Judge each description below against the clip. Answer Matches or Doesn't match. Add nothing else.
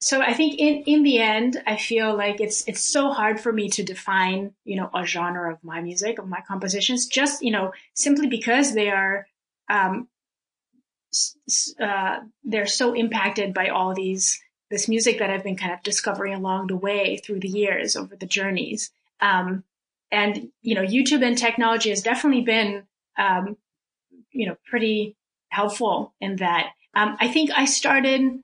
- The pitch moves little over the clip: Doesn't match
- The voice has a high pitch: Matches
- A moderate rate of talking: Matches